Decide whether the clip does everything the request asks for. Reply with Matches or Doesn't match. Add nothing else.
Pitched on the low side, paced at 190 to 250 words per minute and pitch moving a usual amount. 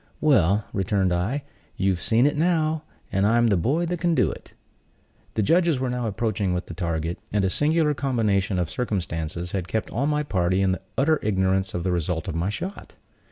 Doesn't match